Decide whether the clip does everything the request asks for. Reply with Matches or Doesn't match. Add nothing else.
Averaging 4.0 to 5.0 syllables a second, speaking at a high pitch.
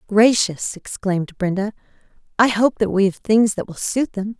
Matches